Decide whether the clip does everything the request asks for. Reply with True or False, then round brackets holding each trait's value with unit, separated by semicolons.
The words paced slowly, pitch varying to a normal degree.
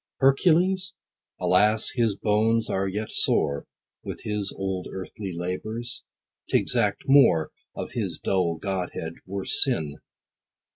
True (115 wpm; 4.3 semitones)